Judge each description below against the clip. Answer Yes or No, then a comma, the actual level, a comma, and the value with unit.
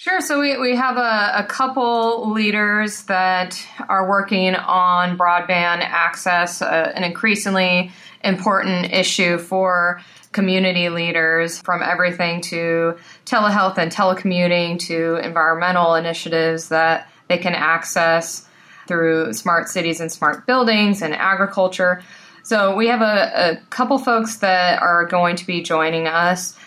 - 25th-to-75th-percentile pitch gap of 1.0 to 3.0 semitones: Yes, average, 2.7 semitones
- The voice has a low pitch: No, medium, 180 Hz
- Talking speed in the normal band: No, slow, 130 wpm